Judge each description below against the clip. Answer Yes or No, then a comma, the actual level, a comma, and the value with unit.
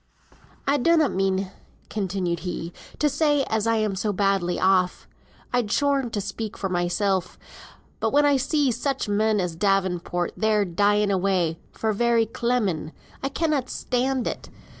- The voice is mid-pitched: No, high, 210 Hz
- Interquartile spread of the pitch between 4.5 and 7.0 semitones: Yes, average, 4.9 semitones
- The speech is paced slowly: No, average, 145 wpm